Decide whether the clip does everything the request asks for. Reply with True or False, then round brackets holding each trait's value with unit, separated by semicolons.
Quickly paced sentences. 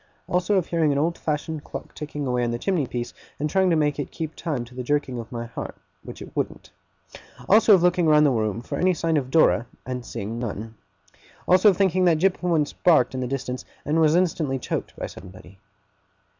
True (215 wpm)